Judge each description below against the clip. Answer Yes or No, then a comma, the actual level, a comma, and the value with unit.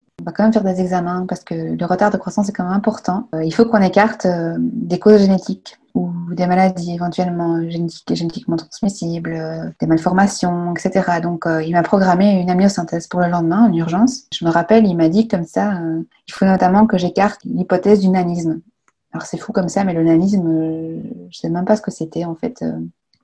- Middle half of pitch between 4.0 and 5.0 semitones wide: No, average, 3.2 semitones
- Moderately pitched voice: Yes, medium, 180 Hz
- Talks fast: No, average, 200 wpm